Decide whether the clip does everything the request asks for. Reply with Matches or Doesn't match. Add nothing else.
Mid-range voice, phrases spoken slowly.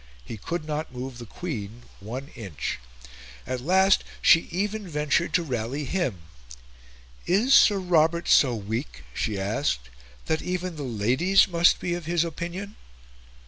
Doesn't match